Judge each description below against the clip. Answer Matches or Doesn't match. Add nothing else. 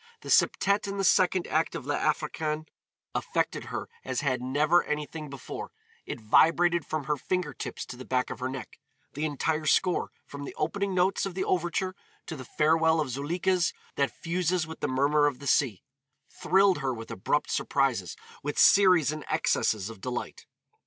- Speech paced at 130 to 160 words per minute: Doesn't match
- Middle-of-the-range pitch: Matches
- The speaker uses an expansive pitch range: Doesn't match